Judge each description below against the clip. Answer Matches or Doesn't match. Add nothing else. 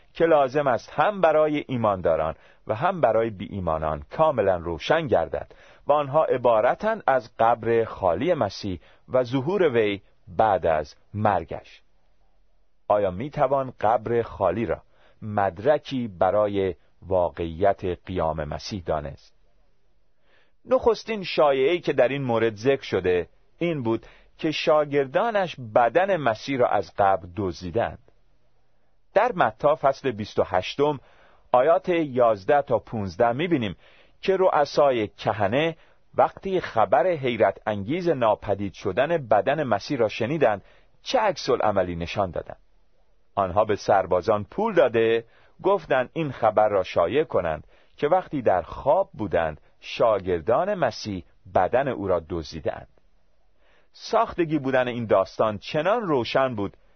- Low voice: Matches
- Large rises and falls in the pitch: Matches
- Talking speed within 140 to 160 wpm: Doesn't match